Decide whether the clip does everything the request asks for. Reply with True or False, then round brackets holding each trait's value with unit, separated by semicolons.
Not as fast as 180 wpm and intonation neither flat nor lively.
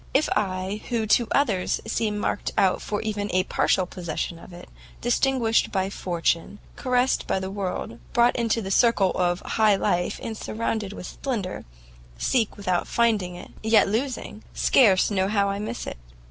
True (165 wpm; 3.6 semitones)